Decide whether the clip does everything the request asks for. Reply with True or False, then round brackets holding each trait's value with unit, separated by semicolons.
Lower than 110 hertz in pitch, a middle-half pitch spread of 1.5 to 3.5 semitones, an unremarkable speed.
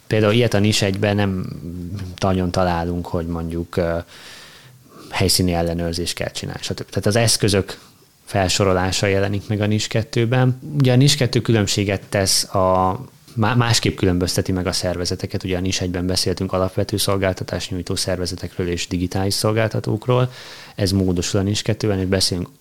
True (100 Hz; 3.1 semitones; 145 wpm)